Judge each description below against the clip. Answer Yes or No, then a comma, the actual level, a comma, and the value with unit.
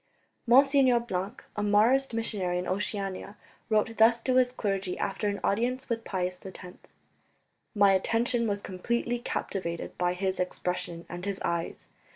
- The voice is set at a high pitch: Yes, high, 205 Hz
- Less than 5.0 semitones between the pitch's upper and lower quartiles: Yes, average, 4.1 semitones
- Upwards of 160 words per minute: No, average, 145 wpm